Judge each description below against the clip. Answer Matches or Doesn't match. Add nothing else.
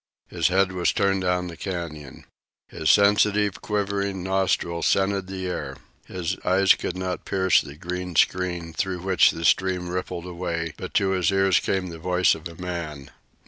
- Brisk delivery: Doesn't match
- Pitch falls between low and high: Doesn't match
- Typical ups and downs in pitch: Doesn't match